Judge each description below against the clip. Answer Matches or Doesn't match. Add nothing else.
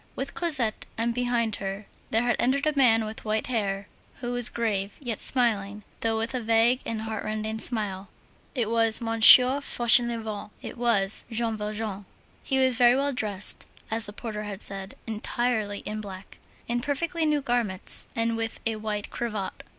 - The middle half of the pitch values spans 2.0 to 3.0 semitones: Matches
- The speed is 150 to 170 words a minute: Matches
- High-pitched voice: Matches